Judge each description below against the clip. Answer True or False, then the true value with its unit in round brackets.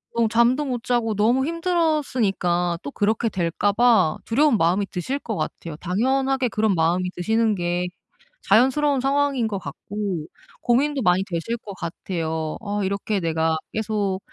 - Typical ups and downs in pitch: False (5.8 semitones)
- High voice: True (210 Hz)